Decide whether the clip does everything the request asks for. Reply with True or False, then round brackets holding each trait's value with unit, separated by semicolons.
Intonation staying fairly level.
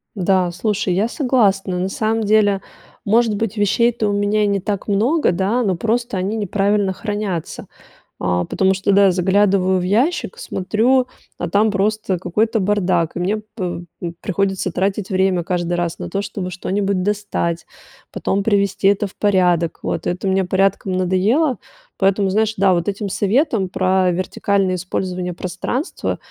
True (2.3 semitones)